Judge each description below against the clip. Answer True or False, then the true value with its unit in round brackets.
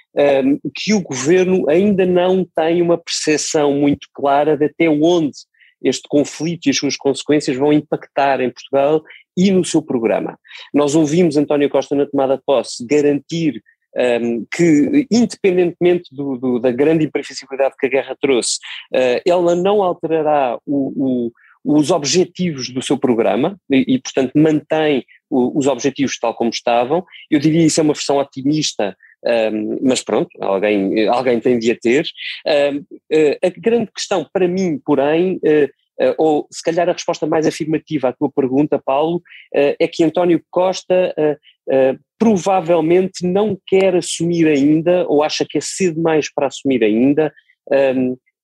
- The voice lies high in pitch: False (150 Hz)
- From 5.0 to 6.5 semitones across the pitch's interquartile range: False (4.2 semitones)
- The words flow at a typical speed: True (160 wpm)